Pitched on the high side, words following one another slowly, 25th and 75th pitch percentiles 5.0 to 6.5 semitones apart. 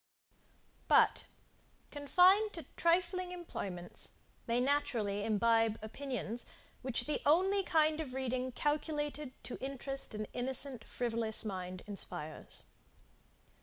Yes: very high, 260 Hz; slow, 100 wpm; wide, 5.5 semitones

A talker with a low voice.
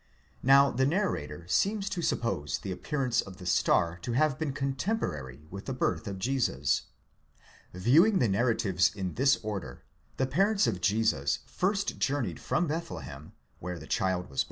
Yes: low, 115 Hz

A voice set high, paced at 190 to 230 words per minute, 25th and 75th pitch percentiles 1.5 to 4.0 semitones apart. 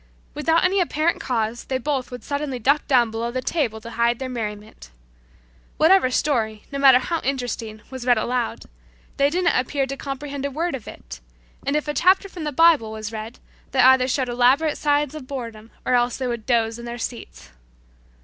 Yes: very high, 255 Hz; average, 195 wpm; average, 3.7 semitones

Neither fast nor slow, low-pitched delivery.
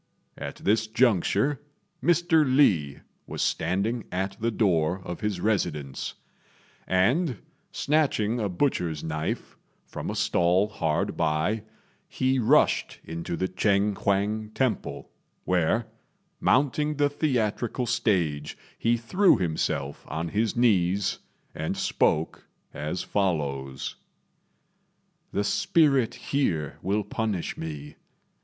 No: slow, 110 wpm; low, 100 Hz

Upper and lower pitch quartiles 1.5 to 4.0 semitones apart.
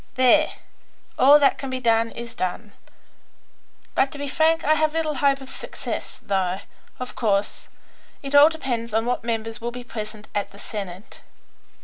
No: average, 4.6 semitones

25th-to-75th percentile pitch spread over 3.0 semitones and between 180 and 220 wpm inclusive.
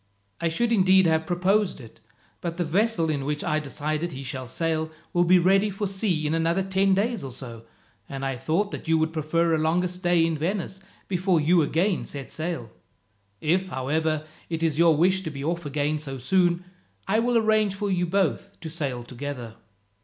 Yes: average, 3.8 semitones; average, 200 wpm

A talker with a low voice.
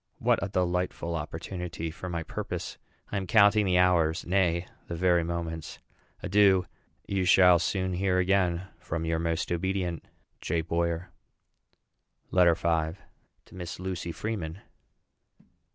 Yes: very low, 90 Hz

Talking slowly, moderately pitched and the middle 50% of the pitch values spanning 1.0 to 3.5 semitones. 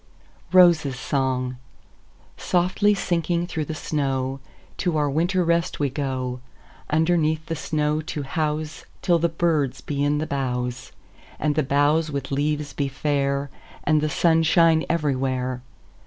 Yes: slow, 115 wpm; medium, 150 Hz; average, 3.1 semitones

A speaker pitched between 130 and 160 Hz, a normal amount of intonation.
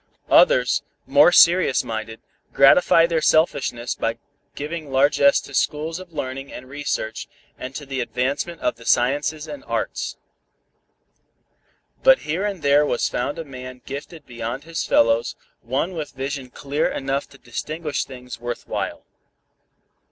Yes: medium, 140 Hz; average, 3.7 semitones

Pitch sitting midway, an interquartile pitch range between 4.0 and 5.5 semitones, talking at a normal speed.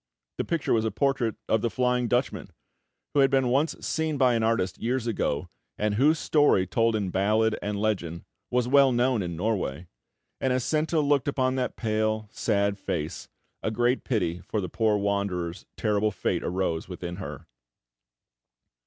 No: low, 110 Hz; average, 4.6 semitones; average, 170 wpm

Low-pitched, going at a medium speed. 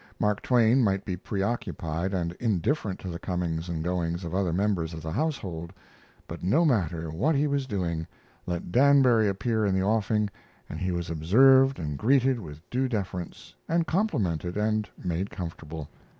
Yes: very low, 95 Hz; average, 165 wpm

